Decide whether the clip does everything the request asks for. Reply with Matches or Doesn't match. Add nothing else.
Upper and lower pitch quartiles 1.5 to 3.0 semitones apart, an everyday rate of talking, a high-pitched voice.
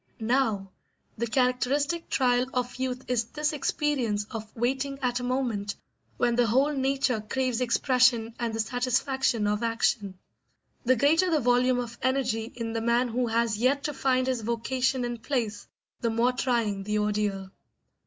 Matches